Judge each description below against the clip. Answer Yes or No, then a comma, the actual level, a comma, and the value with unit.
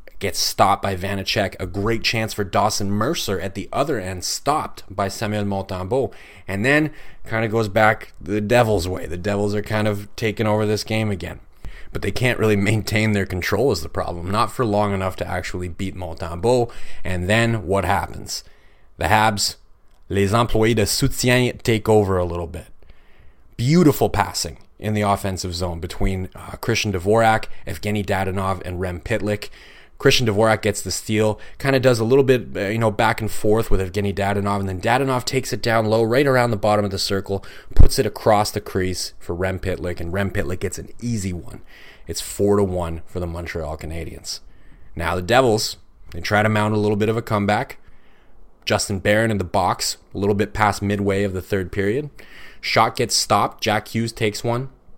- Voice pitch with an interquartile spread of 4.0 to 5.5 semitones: No, average, 2.8 semitones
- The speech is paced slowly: No, average, 190 wpm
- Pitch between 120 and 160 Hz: No, low, 100 Hz